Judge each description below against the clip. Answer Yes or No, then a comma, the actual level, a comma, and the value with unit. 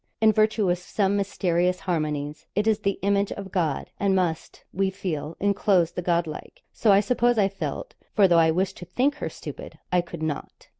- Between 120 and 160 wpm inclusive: No, average, 200 wpm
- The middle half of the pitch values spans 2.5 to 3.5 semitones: Yes, average, 3.1 semitones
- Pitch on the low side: No, high, 190 Hz